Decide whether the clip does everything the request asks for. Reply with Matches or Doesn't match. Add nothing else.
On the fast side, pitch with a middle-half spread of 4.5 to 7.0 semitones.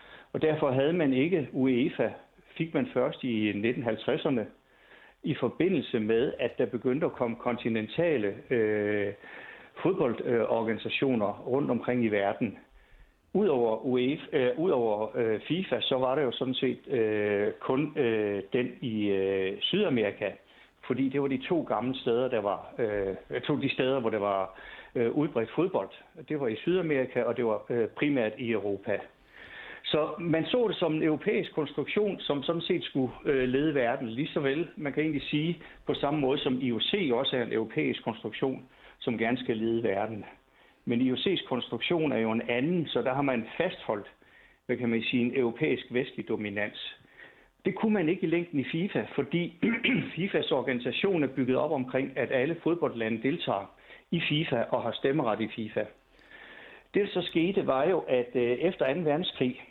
Doesn't match